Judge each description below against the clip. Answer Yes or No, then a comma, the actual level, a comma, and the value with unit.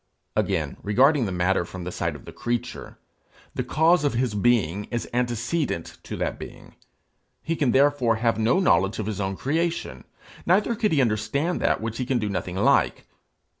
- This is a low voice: Yes, low, 120 Hz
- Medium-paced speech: Yes, average, 180 wpm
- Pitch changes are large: Yes, wide, 5.8 semitones